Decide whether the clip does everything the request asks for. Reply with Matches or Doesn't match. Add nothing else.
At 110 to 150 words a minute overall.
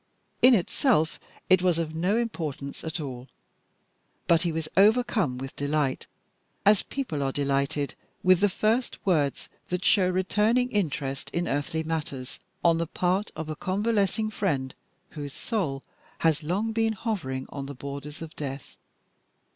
Matches